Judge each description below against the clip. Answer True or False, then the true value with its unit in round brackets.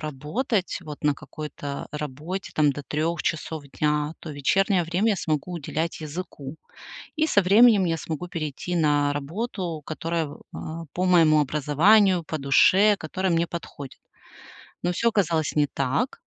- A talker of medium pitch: True (160 Hz)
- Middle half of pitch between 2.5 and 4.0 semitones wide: True (3.6 semitones)